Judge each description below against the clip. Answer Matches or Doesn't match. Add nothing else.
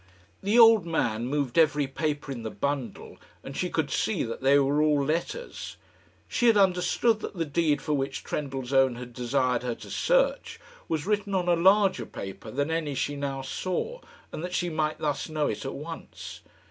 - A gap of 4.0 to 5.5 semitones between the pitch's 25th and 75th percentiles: Matches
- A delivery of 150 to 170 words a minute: Doesn't match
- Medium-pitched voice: Matches